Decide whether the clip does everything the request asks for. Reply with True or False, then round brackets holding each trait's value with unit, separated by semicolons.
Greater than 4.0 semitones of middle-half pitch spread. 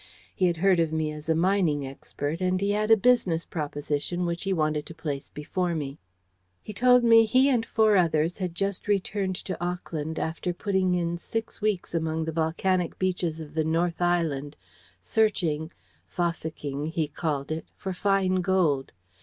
False (3.3 semitones)